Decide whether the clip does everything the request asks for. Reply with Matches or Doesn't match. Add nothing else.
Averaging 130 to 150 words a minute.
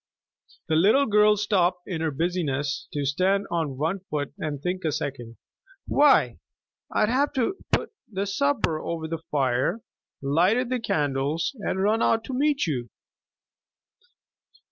Matches